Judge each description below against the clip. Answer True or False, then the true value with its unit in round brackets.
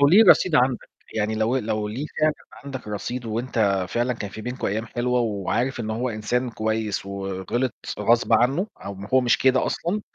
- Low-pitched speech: True (115 Hz)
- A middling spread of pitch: True (3.2 semitones)